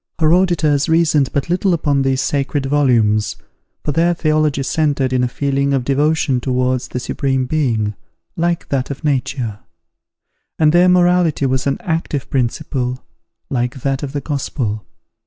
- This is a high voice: No, medium, 140 Hz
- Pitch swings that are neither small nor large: Yes, average, 3.2 semitones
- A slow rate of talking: No, average, 150 wpm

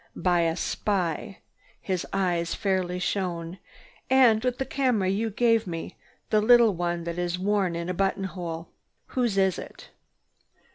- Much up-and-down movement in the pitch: No, average, 3.7 semitones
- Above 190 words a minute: No, average, 150 wpm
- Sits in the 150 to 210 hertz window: Yes, high, 190 Hz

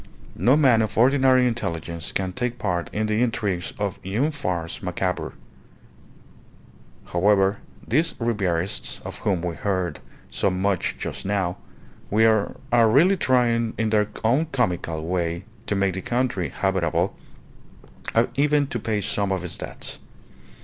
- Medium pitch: No, low, 105 Hz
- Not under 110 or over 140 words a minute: Yes, slow, 135 wpm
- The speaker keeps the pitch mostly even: No, average, 4.8 semitones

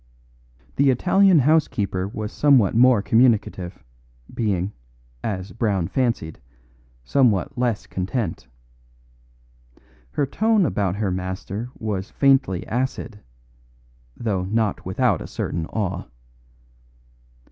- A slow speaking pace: Yes, slow, 95 wpm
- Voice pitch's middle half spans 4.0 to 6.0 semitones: Yes, average, 5.3 semitones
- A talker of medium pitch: No, low, 110 Hz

